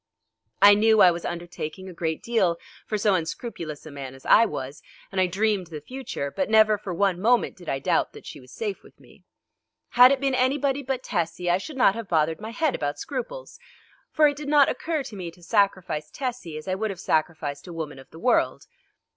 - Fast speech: Yes, fast, 220 wpm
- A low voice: No, high, 195 Hz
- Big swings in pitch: Yes, wide, 6.8 semitones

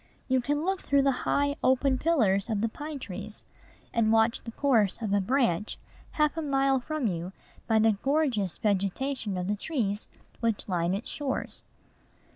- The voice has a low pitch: No, high, 230 Hz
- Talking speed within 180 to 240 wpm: No, average, 170 wpm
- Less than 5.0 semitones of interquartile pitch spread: No, wide, 5.5 semitones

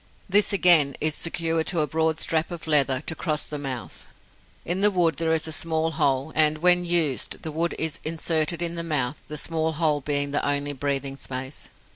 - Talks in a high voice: No, medium, 160 Hz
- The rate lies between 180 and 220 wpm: Yes, average, 200 wpm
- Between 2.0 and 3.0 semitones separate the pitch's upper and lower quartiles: Yes, narrow, 2.6 semitones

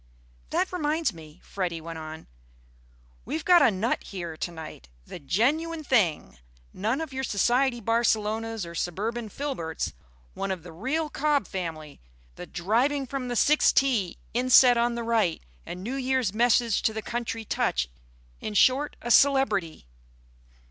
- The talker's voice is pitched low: No, high, 225 Hz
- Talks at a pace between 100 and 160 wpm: Yes, average, 150 wpm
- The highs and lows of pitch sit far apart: Yes, wide, 6.9 semitones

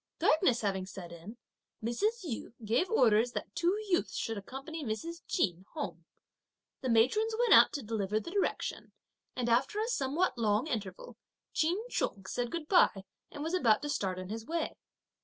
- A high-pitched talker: Yes, very high, 250 Hz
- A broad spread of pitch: Yes, wide, 8.0 semitones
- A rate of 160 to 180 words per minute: Yes, average, 165 wpm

